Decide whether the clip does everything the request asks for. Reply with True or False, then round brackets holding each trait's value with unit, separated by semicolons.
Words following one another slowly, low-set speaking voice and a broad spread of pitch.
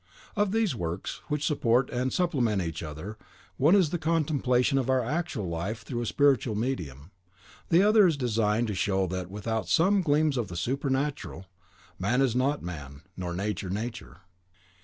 False (165 wpm; 120 Hz; 7.3 semitones)